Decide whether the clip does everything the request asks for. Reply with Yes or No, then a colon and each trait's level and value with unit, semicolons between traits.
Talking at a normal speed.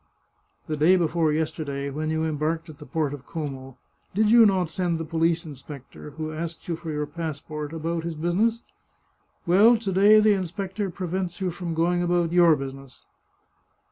Yes: average, 175 wpm